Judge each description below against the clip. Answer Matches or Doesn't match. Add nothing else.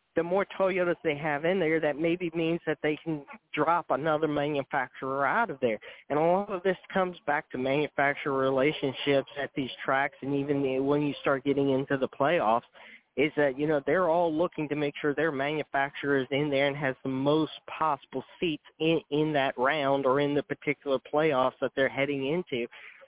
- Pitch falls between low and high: Matches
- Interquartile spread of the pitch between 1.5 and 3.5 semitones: Matches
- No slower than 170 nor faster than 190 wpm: Doesn't match